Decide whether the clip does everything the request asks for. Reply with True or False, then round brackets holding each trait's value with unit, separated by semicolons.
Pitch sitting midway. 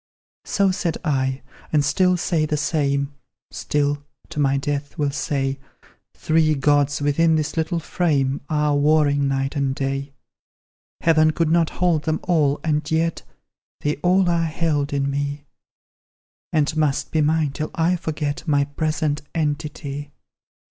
True (150 Hz)